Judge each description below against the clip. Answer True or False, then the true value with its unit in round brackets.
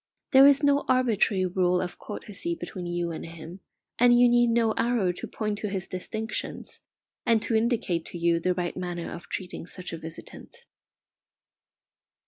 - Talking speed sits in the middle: True (165 wpm)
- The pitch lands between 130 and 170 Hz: False (190 Hz)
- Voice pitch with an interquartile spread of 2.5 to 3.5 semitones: False (5.1 semitones)